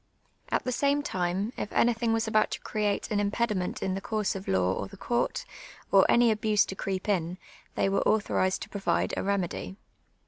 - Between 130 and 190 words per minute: No, average, 200 wpm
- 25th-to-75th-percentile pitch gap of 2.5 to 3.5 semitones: Yes, average, 2.8 semitones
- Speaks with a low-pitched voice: No, high, 205 Hz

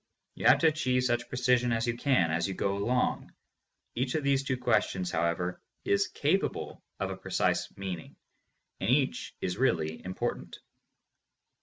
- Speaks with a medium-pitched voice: No, low, 120 Hz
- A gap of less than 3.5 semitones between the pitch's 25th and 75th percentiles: No, wide, 5.6 semitones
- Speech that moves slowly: No, average, 155 wpm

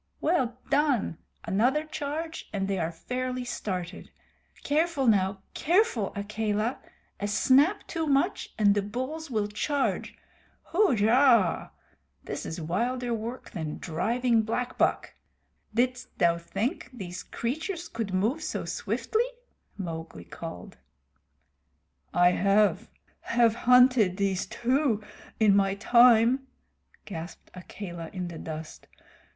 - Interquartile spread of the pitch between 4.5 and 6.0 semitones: Yes, average, 5.1 semitones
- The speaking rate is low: Yes, slow, 115 wpm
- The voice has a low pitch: No, high, 225 Hz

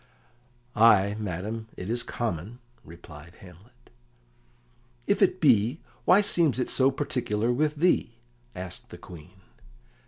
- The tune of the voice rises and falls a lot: Yes, wide, 6.1 semitones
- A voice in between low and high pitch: No, low, 115 Hz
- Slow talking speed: Yes, slow, 120 wpm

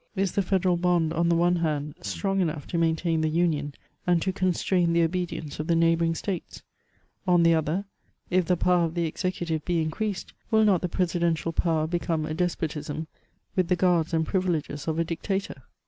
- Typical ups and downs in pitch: No, narrow, 2.0 semitones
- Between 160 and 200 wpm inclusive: Yes, average, 195 wpm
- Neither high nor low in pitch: Yes, medium, 170 Hz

